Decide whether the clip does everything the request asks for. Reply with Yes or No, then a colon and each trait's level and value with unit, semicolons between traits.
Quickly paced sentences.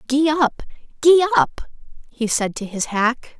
No: average, 160 wpm